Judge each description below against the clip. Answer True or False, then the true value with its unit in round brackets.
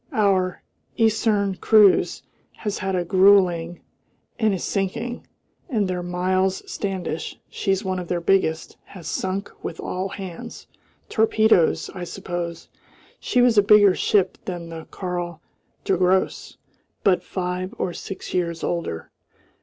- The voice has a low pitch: False (185 Hz)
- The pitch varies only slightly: True (2.2 semitones)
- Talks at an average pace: False (130 wpm)